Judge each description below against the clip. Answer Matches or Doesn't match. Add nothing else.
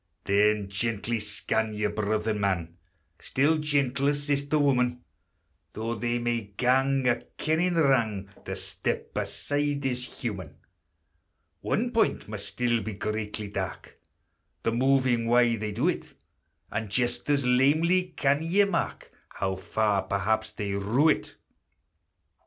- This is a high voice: Doesn't match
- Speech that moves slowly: Matches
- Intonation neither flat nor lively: Matches